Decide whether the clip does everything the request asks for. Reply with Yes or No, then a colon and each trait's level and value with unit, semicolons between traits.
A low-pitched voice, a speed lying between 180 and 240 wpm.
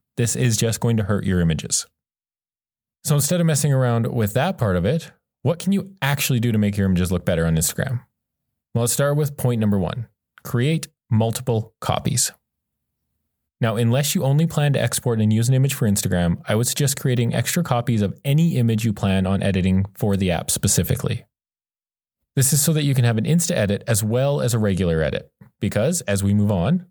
Yes: low, 120 Hz; fast, 205 wpm